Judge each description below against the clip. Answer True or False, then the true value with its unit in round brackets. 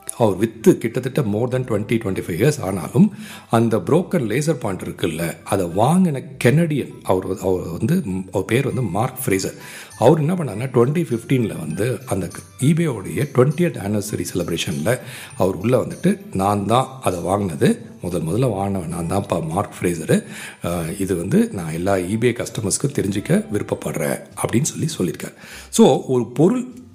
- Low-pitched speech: True (120 Hz)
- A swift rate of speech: True (150 wpm)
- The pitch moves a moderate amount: False (7.1 semitones)